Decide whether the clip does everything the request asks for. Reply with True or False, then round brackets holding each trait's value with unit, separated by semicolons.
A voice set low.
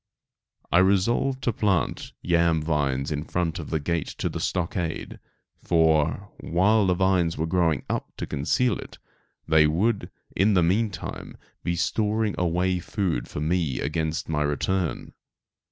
True (85 Hz)